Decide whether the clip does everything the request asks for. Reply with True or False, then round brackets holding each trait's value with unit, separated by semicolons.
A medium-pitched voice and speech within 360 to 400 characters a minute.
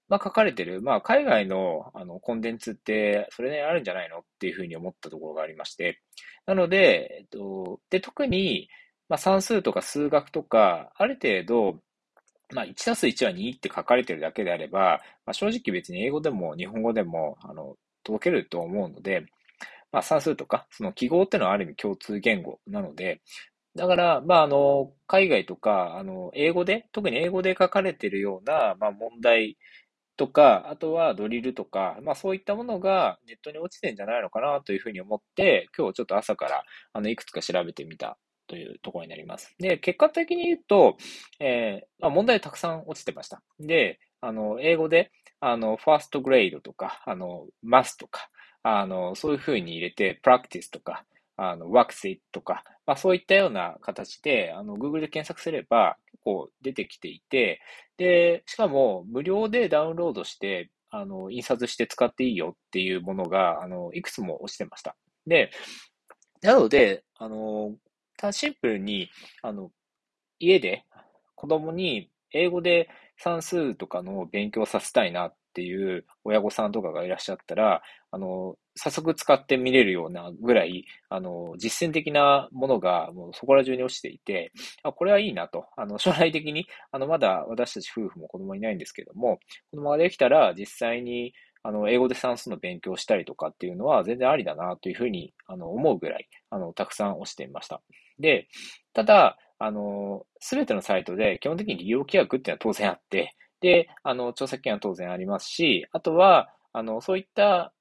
True (155 Hz; 365 characters per minute)